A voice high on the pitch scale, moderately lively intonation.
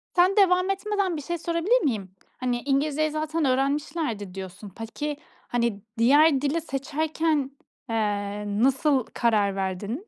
No: very high, 275 Hz; wide, 6.1 semitones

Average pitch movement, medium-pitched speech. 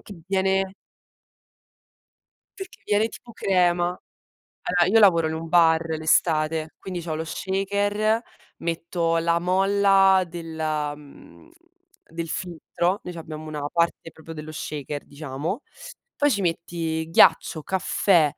Yes: average, 3.2 semitones; medium, 170 Hz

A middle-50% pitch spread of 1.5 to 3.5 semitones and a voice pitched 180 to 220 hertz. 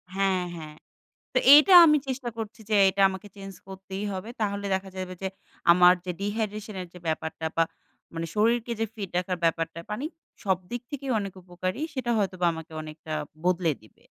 Yes: average, 3.1 semitones; high, 190 Hz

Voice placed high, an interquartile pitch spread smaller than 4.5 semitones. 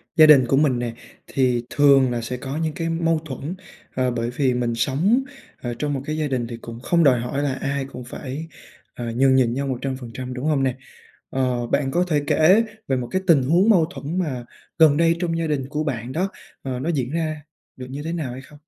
No: low, 135 Hz; average, 3.8 semitones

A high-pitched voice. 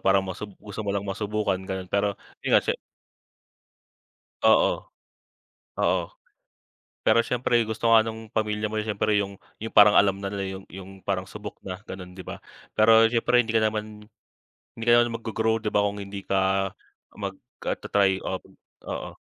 No: low, 105 Hz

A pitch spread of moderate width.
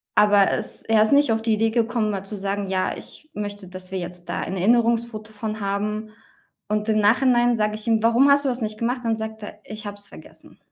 No: narrow, 2.1 semitones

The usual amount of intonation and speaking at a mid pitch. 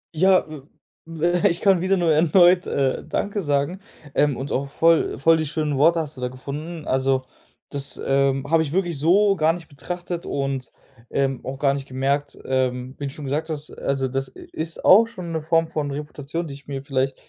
Yes: average, 3.5 semitones; medium, 150 Hz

